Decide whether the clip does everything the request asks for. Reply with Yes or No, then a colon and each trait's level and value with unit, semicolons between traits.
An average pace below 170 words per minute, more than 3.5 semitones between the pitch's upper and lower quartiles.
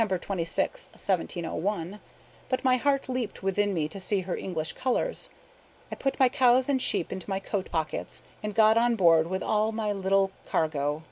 No: average, 175 wpm; average, 5.2 semitones